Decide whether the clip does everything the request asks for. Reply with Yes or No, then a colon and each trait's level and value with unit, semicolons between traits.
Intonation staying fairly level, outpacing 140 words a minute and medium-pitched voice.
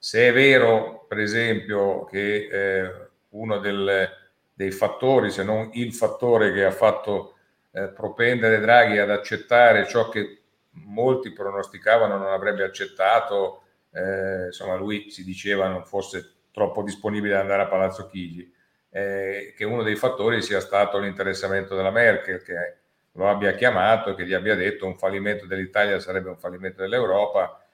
No: narrow, 2.2 semitones; average, 150 wpm; low, 100 Hz